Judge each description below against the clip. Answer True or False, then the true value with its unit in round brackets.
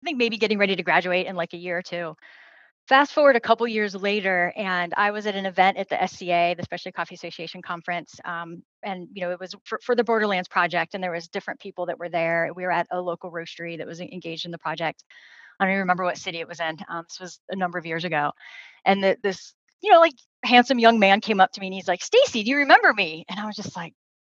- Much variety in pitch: False (3.5 semitones)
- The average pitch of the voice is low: False (185 Hz)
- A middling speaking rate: False (265 wpm)